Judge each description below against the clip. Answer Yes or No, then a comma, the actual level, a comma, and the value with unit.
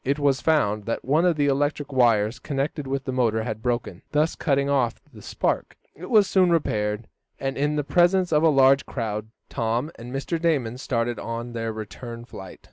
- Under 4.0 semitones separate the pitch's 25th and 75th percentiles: No, average, 4.3 semitones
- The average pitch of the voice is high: No, low, 135 Hz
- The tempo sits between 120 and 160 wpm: No, average, 195 wpm